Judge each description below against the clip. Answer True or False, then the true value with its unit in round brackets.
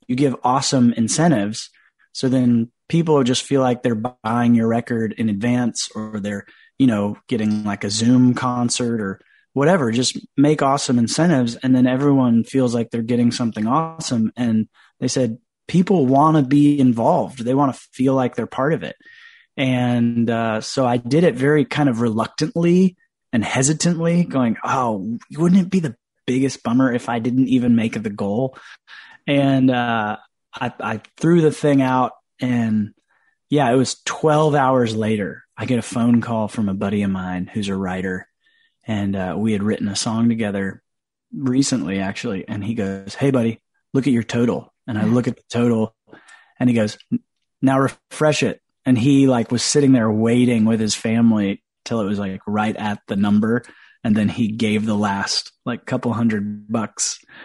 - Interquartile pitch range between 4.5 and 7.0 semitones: False (3.7 semitones)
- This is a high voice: False (120 Hz)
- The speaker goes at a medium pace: True (180 wpm)